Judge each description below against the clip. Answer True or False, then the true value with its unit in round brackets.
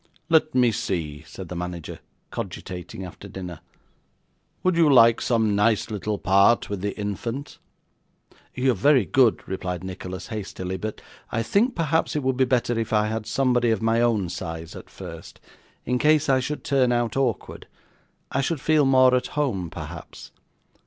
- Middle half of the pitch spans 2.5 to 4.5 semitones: False (5.5 semitones)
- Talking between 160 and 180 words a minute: True (165 wpm)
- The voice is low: True (115 Hz)